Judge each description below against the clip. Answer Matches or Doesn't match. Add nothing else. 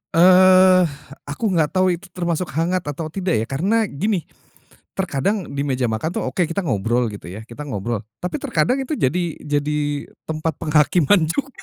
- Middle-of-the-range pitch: Matches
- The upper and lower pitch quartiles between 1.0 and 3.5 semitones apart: Doesn't match